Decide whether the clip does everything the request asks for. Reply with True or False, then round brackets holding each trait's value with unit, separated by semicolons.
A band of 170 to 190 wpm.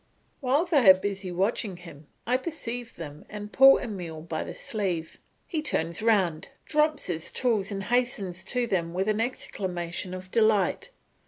False (160 wpm)